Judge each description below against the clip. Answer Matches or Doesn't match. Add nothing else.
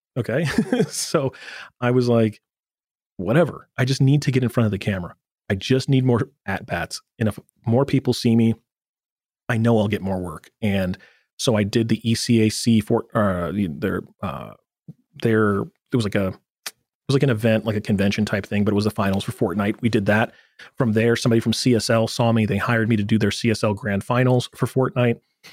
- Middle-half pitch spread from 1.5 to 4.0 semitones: Matches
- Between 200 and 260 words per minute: Matches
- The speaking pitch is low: Matches